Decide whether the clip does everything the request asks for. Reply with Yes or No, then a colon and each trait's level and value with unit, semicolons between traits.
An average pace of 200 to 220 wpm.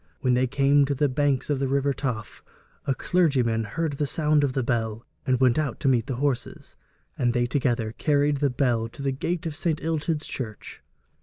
Yes: fast, 205 wpm